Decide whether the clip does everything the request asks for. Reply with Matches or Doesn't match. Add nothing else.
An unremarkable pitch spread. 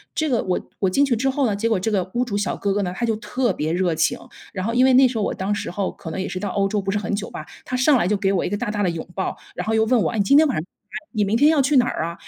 Matches